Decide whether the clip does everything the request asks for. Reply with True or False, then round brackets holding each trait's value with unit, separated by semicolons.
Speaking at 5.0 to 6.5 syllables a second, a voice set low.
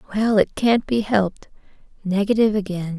False (5.6 syllables/s; 205 Hz)